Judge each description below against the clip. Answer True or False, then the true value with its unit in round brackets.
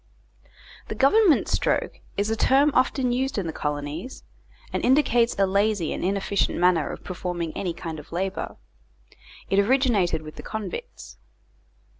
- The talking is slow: False (145 wpm)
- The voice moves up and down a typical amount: False (6.5 semitones)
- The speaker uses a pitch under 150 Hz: False (195 Hz)